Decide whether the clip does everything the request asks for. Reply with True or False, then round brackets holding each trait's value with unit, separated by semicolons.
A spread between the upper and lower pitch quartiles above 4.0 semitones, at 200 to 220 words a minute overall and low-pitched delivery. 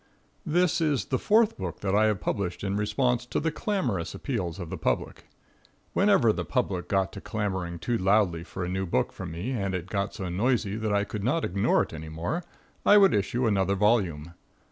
True (5.1 semitones; 205 wpm; 100 Hz)